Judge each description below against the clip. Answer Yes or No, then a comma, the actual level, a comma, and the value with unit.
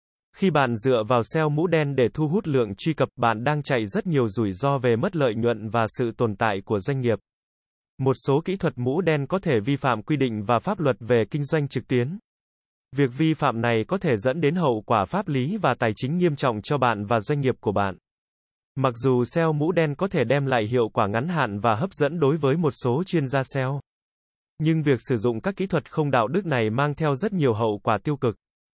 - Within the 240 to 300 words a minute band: Yes, average, 245 wpm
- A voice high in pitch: No, low, 135 Hz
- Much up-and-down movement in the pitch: No, average, 4.7 semitones